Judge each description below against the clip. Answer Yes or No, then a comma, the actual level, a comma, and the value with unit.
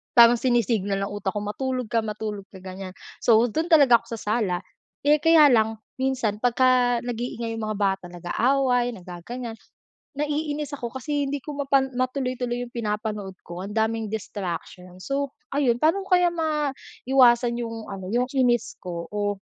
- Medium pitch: No, high, 235 Hz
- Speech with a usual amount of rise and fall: Yes, average, 4.3 semitones